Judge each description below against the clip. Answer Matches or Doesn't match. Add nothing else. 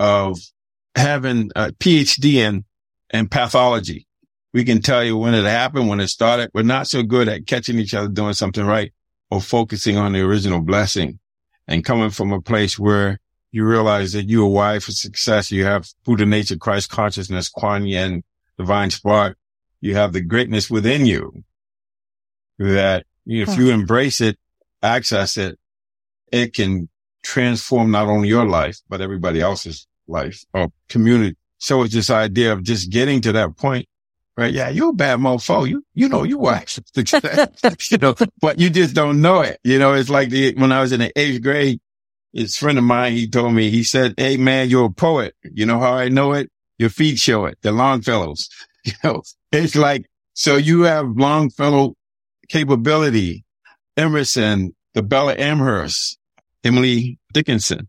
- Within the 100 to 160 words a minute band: Doesn't match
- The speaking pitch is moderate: Doesn't match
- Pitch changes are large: Doesn't match